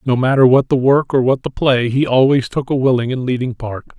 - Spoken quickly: Yes, fast, 255 wpm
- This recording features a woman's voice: No, male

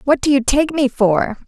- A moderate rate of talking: No, fast, 245 wpm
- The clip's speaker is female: Yes, female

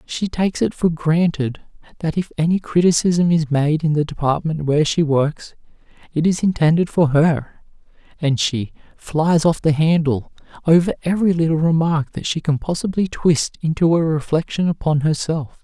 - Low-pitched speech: No, medium, 160 Hz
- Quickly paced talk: No, average, 160 wpm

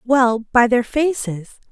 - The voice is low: No, high, 240 Hz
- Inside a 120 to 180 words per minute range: Yes, average, 140 wpm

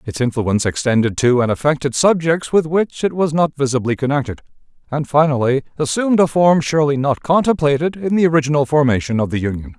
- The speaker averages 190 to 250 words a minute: No, average, 180 wpm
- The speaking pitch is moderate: Yes, medium, 145 Hz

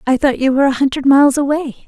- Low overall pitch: No, very high, 275 Hz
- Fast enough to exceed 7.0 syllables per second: Yes, 7.3 syllables/s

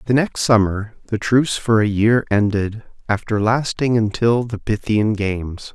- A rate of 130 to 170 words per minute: Yes, average, 155 wpm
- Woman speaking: No, male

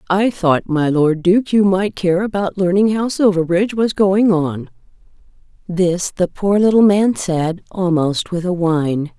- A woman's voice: Yes, female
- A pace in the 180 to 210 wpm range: No, average, 165 wpm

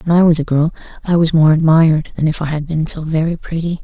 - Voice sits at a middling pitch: Yes, medium, 160 Hz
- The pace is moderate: No, fast, 265 wpm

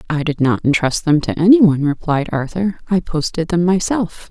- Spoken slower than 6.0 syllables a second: Yes, 5.3 syllables/s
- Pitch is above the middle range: No, medium, 165 Hz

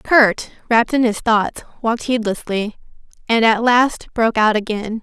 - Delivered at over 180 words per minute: No, average, 155 wpm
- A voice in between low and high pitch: No, high, 225 Hz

